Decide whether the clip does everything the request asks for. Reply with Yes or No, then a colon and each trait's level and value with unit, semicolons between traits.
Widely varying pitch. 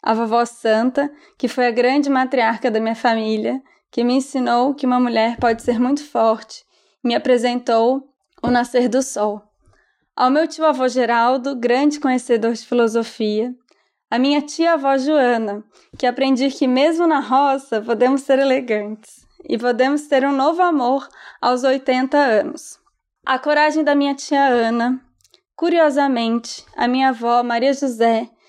No: average, 2.8 semitones